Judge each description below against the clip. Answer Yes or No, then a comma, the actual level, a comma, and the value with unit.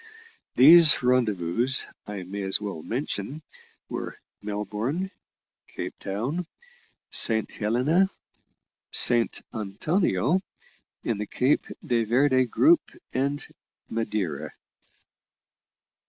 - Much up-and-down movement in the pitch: Yes, wide, 5.8 semitones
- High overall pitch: No, low, 120 Hz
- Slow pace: Yes, slow, 85 wpm